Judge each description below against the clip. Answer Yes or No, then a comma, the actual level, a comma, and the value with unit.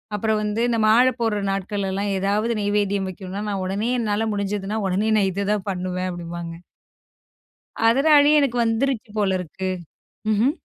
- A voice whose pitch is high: Yes, high, 205 Hz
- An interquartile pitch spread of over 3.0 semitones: No, average, 2.7 semitones